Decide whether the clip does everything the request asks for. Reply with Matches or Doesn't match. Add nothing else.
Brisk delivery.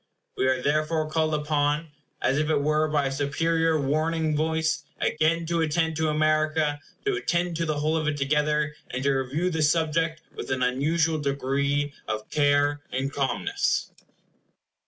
Doesn't match